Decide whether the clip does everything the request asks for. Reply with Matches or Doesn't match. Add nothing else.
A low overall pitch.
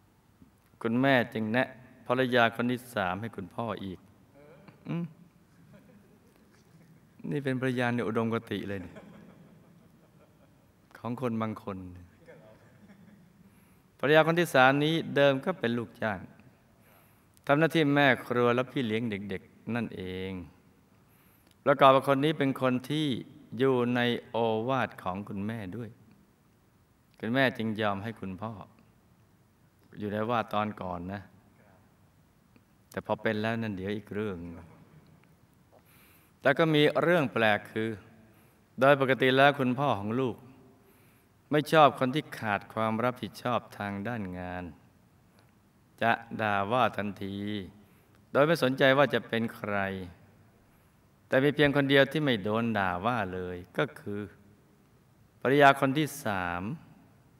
Matches